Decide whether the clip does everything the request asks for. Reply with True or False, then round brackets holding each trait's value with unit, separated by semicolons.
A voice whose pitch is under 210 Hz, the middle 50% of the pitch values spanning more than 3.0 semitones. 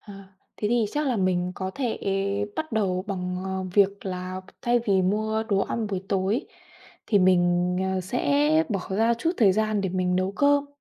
True (200 Hz; 3.7 semitones)